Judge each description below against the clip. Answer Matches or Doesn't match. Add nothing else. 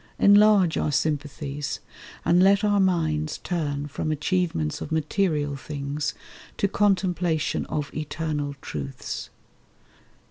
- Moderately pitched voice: Matches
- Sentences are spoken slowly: Matches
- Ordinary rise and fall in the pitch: Matches